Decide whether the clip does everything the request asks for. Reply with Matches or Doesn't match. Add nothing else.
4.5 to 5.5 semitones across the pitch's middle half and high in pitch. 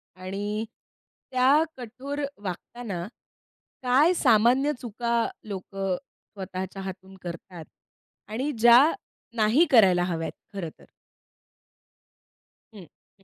Matches